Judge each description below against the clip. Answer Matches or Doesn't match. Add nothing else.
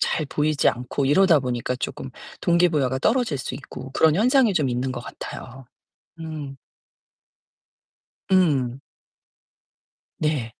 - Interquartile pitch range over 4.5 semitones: Doesn't match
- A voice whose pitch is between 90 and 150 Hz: Matches